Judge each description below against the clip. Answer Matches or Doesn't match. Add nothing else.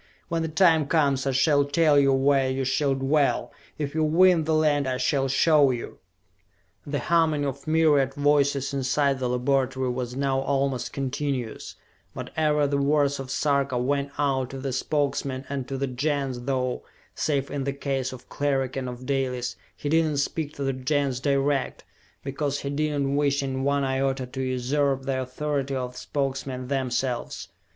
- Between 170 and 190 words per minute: Matches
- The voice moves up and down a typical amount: Doesn't match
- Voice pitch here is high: Doesn't match